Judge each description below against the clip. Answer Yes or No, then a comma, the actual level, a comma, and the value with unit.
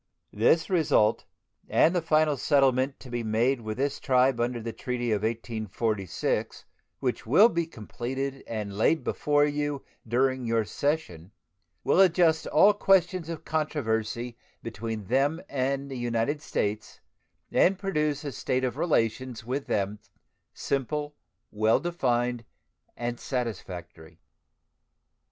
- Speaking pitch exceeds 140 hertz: No, low, 130 Hz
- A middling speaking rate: No, slow, 125 wpm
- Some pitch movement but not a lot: Yes, average, 4.8 semitones